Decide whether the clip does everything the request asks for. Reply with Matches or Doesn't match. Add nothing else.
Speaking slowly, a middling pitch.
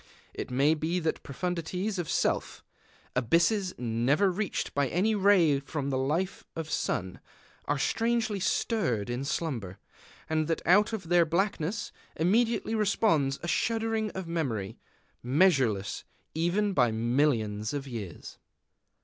Matches